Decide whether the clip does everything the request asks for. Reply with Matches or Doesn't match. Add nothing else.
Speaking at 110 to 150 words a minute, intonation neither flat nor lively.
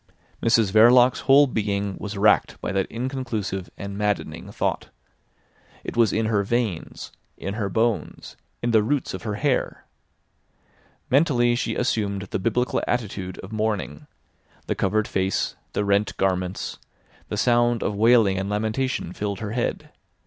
Matches